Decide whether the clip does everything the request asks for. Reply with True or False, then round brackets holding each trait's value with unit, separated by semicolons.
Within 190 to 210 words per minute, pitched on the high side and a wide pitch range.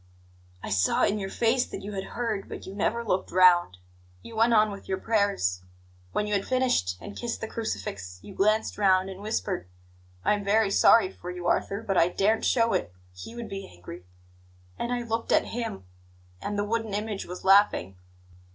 False (195 wpm; 200 Hz; 3.3 semitones)